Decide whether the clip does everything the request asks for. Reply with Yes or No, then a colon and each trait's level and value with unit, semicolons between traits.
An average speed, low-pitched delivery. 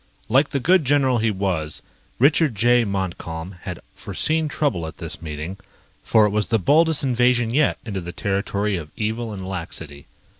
Yes: average, 165 wpm; low, 105 Hz